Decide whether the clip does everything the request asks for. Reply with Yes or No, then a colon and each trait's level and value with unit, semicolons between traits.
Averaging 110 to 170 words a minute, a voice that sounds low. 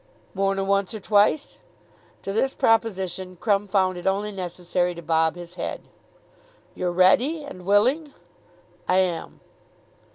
No: slow, 135 wpm; high, 195 Hz